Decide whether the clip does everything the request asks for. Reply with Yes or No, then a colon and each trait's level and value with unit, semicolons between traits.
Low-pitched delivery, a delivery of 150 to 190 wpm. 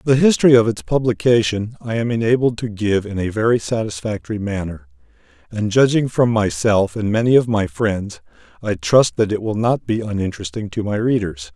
Yes: low, 110 Hz; average, 180 wpm